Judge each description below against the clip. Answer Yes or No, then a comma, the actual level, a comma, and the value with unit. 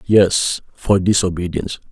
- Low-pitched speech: Yes, very low, 95 Hz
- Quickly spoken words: No, slow, 95 wpm